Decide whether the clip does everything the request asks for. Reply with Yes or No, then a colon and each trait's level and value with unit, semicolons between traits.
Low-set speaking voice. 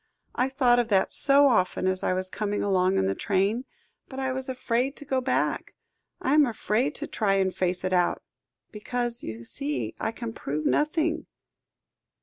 No: high, 230 Hz